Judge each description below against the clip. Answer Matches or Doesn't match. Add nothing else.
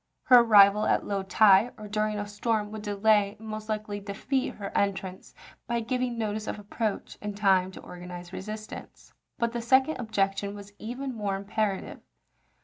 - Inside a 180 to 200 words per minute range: Doesn't match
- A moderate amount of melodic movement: Doesn't match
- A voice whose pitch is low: Doesn't match